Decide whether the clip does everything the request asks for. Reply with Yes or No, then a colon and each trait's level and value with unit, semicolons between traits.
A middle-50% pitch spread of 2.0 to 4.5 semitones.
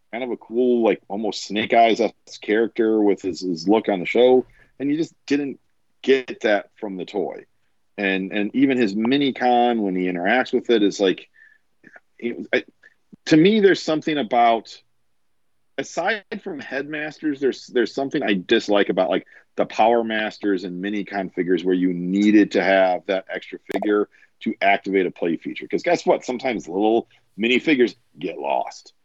No: average, 5.1 semitones